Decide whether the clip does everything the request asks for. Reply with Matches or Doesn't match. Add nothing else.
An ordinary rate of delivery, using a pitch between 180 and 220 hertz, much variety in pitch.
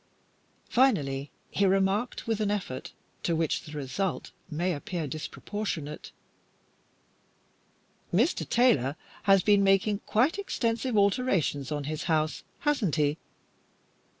Doesn't match